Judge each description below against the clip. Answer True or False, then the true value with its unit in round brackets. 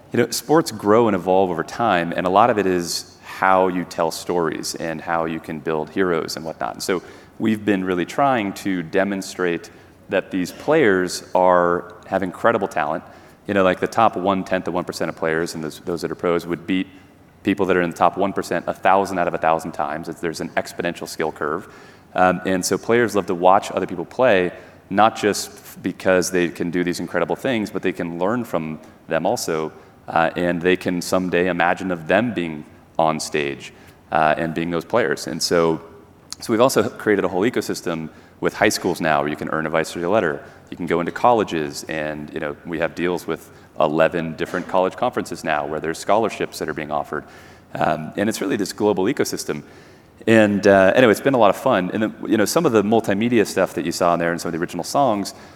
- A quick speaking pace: True (220 wpm)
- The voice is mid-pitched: False (90 Hz)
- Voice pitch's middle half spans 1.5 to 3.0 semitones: True (2.4 semitones)